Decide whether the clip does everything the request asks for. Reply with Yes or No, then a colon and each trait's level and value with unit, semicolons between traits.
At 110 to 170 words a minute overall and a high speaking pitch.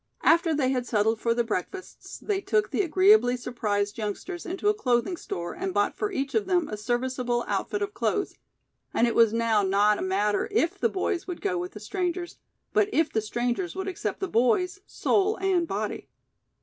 No: average, 195 wpm; very high, 260 Hz